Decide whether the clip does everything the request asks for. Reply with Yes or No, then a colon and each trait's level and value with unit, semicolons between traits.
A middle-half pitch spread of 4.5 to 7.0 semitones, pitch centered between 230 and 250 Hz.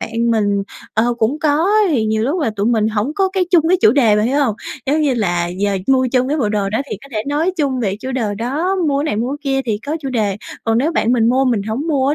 Yes: average, 5.0 semitones; high, 245 Hz